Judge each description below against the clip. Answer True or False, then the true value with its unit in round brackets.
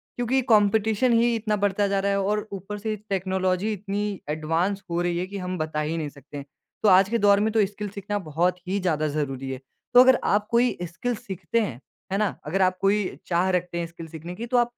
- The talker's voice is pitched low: False (195 Hz)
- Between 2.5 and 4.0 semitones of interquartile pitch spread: True (3.4 semitones)